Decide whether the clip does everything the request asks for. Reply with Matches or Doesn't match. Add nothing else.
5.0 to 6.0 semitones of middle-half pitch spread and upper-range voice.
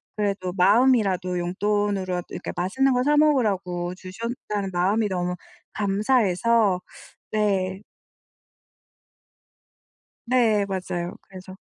Doesn't match